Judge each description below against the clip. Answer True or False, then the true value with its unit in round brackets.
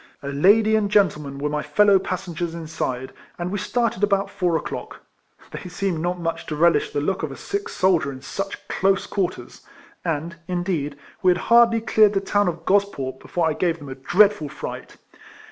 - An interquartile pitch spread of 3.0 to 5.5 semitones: True (4.2 semitones)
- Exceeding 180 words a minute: True (190 wpm)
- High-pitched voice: False (180 Hz)